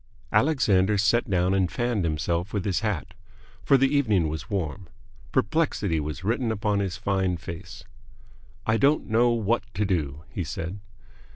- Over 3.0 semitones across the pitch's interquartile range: Yes, average, 4.3 semitones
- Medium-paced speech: Yes, average, 155 wpm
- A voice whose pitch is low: Yes, low, 100 Hz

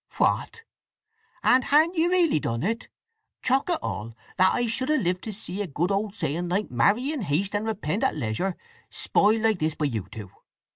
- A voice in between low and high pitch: No, high, 205 Hz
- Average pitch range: No, wide, 8.3 semitones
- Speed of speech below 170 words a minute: No, average, 190 wpm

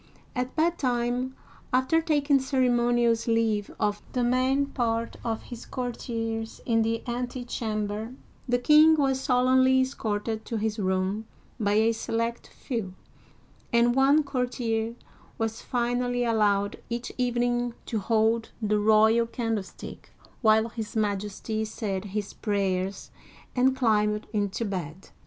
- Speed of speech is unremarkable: No, slow, 120 wpm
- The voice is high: Yes, high, 230 Hz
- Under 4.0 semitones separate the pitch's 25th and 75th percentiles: Yes, narrow, 2.5 semitones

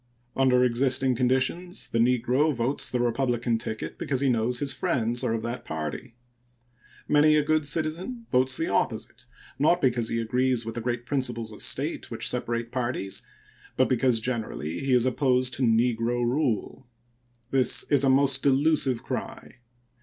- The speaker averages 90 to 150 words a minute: No, average, 160 wpm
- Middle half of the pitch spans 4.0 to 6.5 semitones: No, narrow, 2.5 semitones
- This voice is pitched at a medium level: No, low, 125 Hz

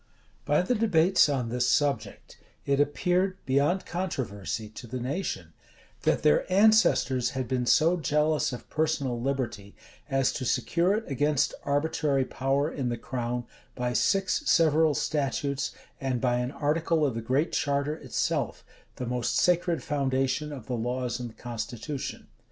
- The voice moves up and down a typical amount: Yes, average, 4.1 semitones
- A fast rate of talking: No, average, 145 wpm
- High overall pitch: No, medium, 140 Hz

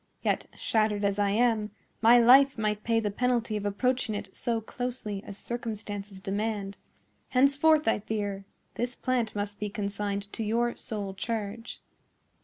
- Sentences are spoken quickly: No, average, 150 wpm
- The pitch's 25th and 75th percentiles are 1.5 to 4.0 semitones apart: Yes, average, 2.8 semitones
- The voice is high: Yes, high, 215 Hz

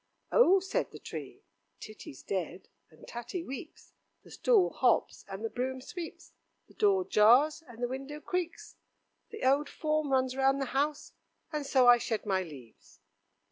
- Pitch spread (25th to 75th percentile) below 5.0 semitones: No, wide, 5.4 semitones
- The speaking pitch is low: No, very high, 265 Hz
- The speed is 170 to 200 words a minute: No, average, 160 wpm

